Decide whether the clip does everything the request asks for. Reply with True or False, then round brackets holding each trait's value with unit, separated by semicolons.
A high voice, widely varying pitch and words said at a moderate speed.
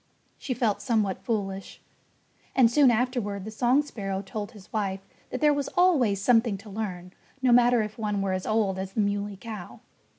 False (215 Hz; 3.7 semitones; 185 wpm)